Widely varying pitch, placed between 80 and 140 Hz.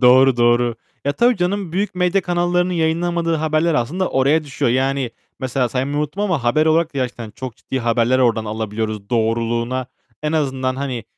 Yes: wide, 5.7 semitones; low, 135 Hz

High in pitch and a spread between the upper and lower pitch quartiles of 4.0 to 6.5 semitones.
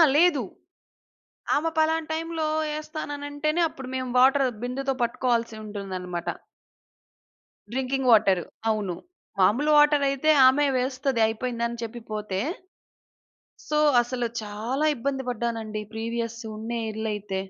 Yes: very high, 250 Hz; average, 4.7 semitones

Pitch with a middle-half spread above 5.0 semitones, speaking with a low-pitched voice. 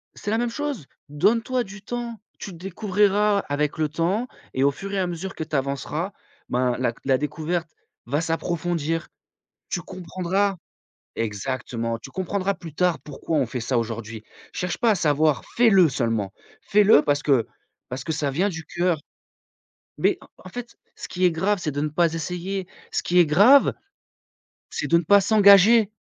No: wide, 5.5 semitones; medium, 170 Hz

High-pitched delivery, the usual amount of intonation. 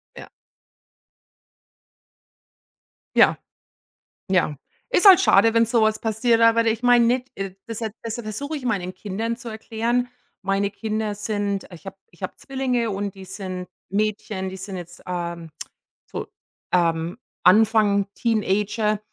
Yes: high, 215 Hz; average, 3.1 semitones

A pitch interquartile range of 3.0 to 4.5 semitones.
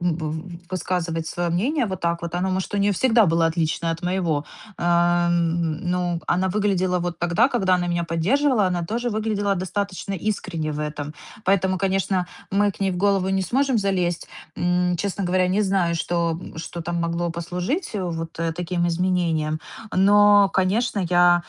No: narrow, 2.5 semitones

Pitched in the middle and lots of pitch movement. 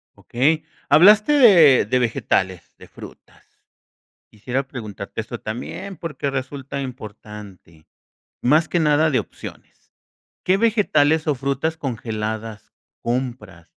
No: low, 130 Hz; wide, 6.0 semitones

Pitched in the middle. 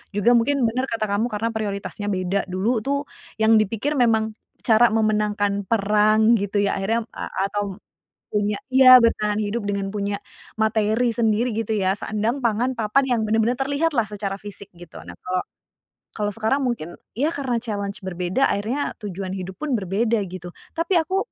No: high, 215 Hz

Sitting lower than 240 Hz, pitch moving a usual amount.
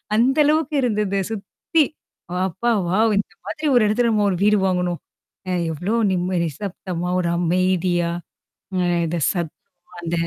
Yes: high, 190 Hz; average, 4.0 semitones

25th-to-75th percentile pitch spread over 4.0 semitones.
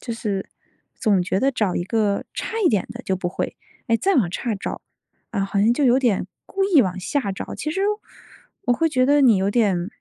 Yes: average, 5.2 semitones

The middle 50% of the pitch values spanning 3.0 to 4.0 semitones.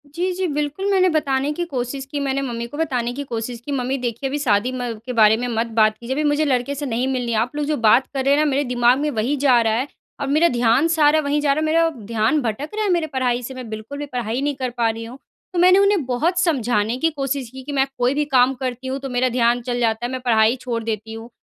Yes: average, 3.6 semitones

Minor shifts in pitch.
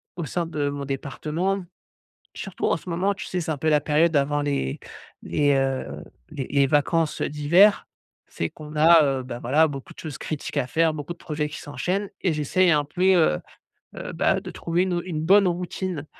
No: average, 3.3 semitones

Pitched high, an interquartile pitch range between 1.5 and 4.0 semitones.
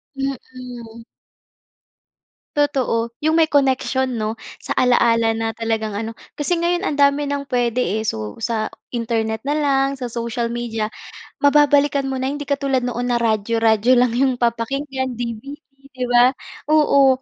Yes: very high, 250 Hz; average, 3.3 semitones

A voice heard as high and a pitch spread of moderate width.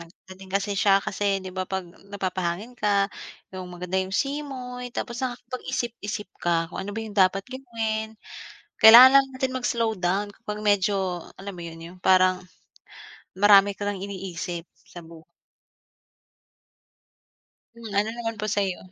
Yes: high, 200 Hz; average, 3.4 semitones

